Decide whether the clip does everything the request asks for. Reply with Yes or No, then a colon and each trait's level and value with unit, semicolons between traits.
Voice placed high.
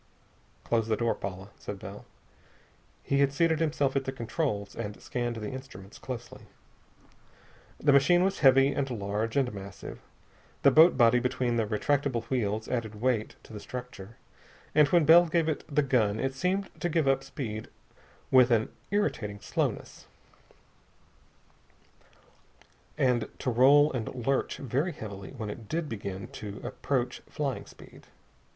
No: low, 125 Hz